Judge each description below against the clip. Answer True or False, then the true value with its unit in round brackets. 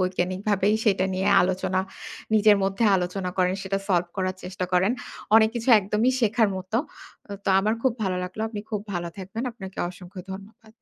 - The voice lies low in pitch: False (190 Hz)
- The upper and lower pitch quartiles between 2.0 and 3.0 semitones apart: True (2.5 semitones)